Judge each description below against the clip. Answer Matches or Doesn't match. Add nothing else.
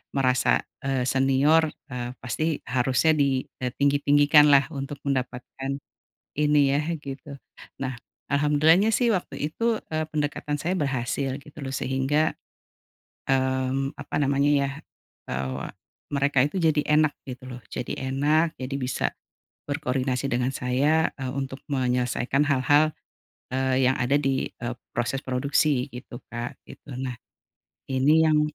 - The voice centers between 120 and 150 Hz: Matches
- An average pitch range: Doesn't match